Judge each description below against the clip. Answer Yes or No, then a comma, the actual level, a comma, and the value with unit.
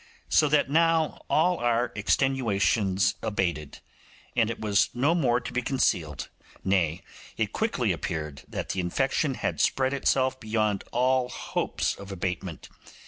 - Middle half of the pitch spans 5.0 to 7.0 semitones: Yes, wide, 5.6 semitones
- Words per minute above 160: No, average, 140 wpm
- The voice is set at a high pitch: No, low, 115 Hz